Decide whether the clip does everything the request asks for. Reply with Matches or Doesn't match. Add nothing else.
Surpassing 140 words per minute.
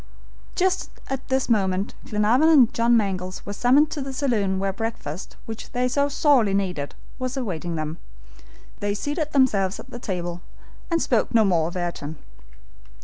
Matches